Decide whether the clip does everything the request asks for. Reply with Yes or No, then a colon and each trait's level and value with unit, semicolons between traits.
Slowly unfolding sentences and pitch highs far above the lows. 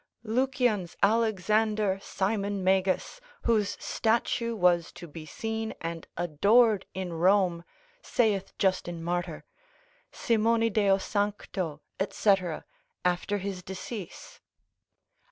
No: slow, 95 wpm; average, 3.6 semitones